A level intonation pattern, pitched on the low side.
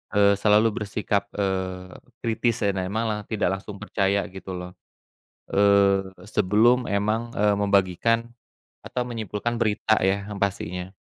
Yes: narrow, 2.1 semitones; low, 100 Hz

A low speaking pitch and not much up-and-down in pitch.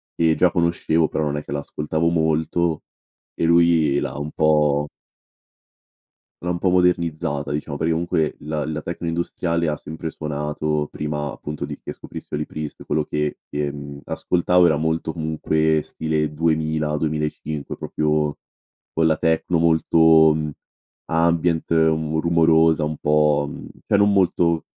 Yes: very low, 80 Hz; narrow, 1.6 semitones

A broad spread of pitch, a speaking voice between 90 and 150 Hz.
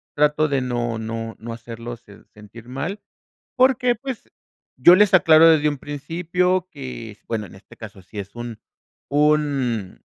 Yes: wide, 6.3 semitones; low, 135 Hz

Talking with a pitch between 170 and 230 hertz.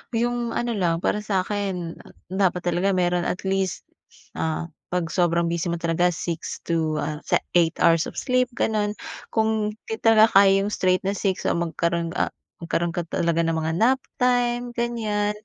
Yes: medium, 185 Hz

